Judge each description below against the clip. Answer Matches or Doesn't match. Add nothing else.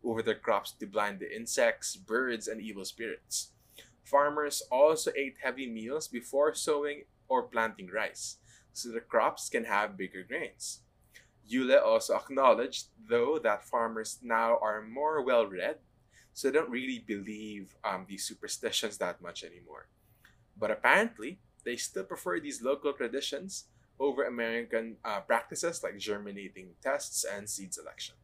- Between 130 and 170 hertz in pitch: Doesn't match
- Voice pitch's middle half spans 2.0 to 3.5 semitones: Doesn't match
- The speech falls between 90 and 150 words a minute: Matches